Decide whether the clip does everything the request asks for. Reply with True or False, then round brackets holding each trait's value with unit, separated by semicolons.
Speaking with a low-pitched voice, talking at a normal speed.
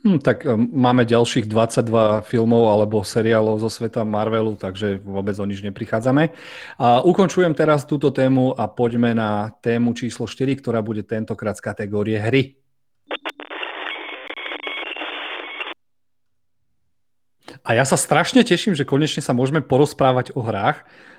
True (120 Hz; 125 wpm)